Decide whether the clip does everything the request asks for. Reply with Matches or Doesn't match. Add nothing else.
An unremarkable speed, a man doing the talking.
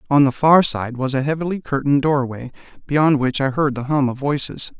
Doesn't match